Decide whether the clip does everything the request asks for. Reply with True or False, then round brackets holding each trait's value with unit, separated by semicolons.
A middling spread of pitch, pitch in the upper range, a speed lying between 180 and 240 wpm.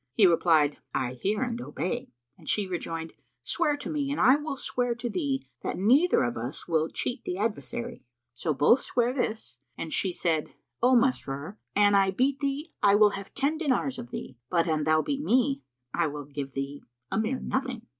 False (8.5 semitones; 210 Hz; 195 wpm)